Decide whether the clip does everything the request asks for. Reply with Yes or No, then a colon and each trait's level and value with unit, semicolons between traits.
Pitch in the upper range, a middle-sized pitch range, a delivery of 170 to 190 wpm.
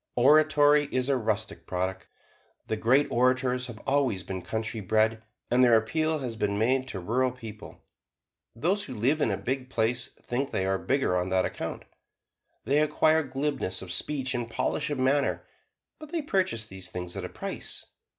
No: low, 125 Hz; average, 4.6 semitones; average, 175 wpm